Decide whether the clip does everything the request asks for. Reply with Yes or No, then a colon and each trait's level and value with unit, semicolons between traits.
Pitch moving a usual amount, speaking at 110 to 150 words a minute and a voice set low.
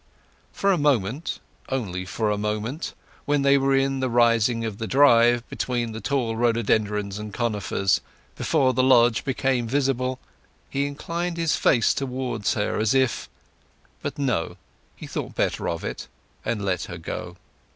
Yes: average, 4.1 semitones; average, 145 wpm; low, 120 Hz